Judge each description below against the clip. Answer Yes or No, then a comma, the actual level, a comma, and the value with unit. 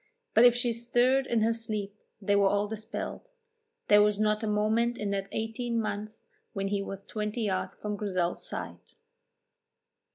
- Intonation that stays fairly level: Yes, narrow, 2.2 semitones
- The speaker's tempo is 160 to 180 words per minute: Yes, average, 165 wpm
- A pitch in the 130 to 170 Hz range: No, high, 215 Hz